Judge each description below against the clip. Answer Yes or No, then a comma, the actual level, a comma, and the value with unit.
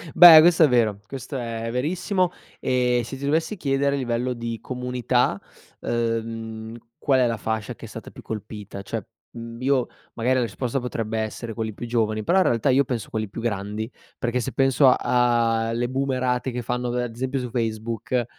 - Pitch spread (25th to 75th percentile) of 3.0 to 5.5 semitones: No, narrow, 2.4 semitones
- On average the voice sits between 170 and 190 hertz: No, low, 120 Hz